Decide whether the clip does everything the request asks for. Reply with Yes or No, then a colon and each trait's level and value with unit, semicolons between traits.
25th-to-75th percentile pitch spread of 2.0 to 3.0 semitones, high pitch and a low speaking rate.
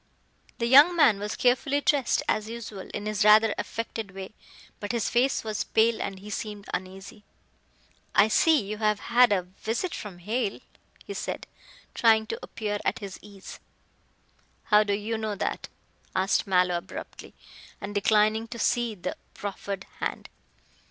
No: narrow, 2.5 semitones; high, 215 Hz; average, 155 wpm